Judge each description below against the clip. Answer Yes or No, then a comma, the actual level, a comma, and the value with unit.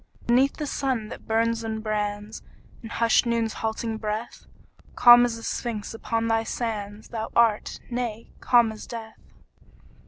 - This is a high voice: Yes, high, 225 Hz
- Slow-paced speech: No, average, 150 wpm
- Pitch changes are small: Yes, narrow, 1.4 semitones